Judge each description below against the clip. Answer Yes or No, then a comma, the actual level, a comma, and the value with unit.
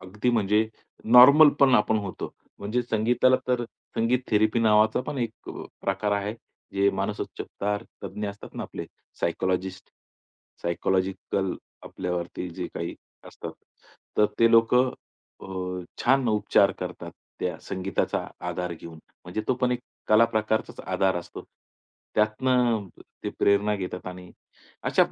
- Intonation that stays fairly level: No, average, 3.6 semitones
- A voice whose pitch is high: No, low, 105 Hz